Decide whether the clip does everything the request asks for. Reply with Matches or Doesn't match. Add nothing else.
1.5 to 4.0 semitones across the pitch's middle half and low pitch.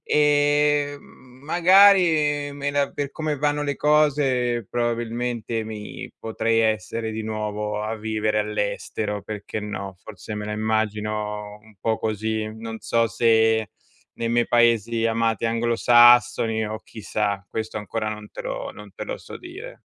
Doesn't match